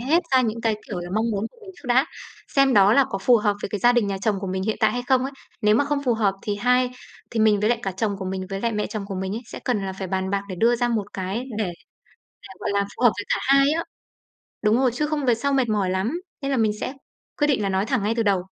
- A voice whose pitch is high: Yes, high, 220 Hz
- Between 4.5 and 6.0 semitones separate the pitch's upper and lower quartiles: No, average, 4.0 semitones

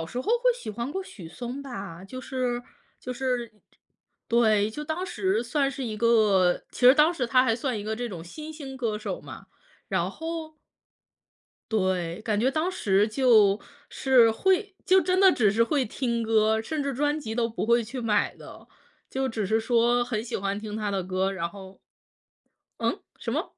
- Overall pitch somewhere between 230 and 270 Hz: Yes, high, 235 Hz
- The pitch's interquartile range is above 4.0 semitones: Yes, average, 4.5 semitones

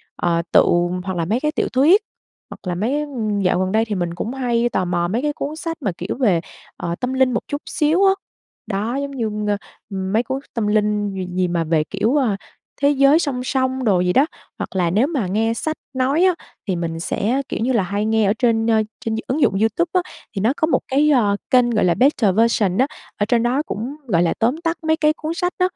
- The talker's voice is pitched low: No, high, 230 Hz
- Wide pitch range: Yes, wide, 5.8 semitones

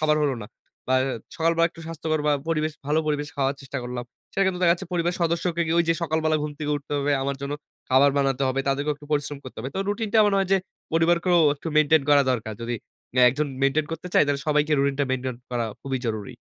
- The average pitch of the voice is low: No, medium, 150 Hz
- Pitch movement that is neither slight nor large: Yes, average, 3.3 semitones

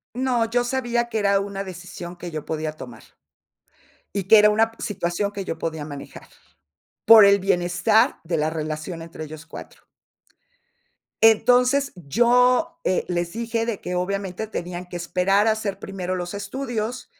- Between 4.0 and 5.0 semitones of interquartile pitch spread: Yes, average, 4.6 semitones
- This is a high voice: Yes, high, 195 Hz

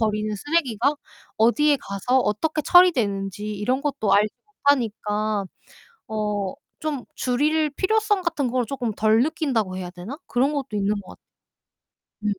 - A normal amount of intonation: No, wide, 5.7 semitones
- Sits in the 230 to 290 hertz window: Yes, high, 235 Hz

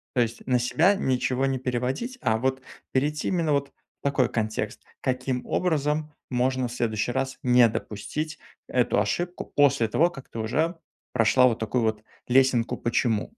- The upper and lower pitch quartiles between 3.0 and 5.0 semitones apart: Yes, average, 3.3 semitones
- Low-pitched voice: Yes, low, 130 Hz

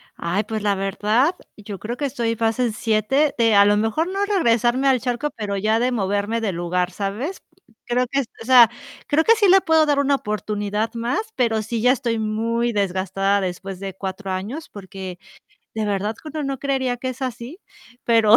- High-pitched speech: Yes, high, 225 Hz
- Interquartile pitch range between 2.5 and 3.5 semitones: No, average, 4.2 semitones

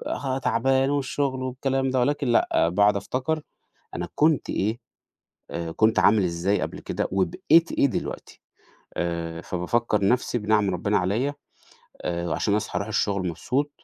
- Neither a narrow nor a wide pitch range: No, wide, 6.1 semitones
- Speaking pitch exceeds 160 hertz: No, low, 110 Hz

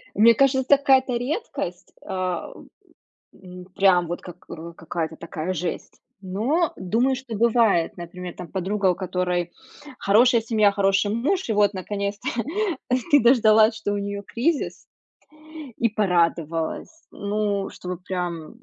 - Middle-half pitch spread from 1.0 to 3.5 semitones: No, average, 4.3 semitones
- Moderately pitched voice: No, high, 200 Hz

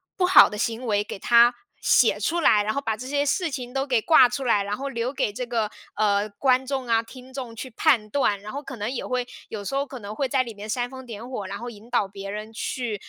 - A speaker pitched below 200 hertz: No, high, 240 Hz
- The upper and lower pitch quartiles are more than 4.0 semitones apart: No, average, 3.7 semitones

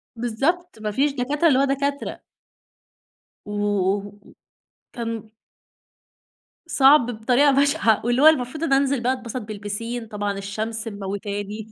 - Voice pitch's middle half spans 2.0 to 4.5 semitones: No, average, 5.0 semitones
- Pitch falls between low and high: No, high, 235 Hz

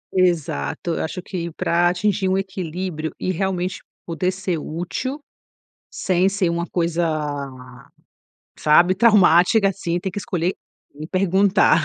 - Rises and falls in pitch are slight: Yes, narrow, 2.2 semitones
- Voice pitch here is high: No, medium, 180 Hz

